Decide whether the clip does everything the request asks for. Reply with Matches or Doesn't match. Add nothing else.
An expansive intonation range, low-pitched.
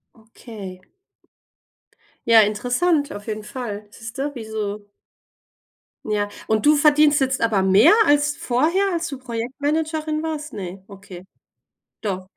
Doesn't match